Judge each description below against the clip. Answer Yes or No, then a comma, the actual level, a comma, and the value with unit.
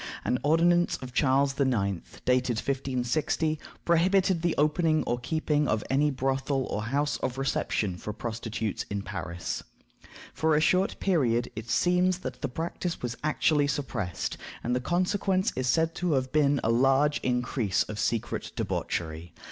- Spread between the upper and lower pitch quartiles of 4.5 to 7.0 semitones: Yes, average, 4.9 semitones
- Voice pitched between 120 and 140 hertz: Yes, low, 135 Hz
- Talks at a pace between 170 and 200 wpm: No, average, 150 wpm